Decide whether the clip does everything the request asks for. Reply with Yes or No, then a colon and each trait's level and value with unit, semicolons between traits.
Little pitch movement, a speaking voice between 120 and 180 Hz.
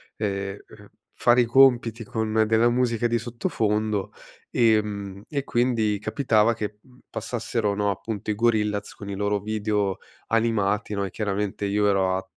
No: narrow, 2.2 semitones; low, 105 Hz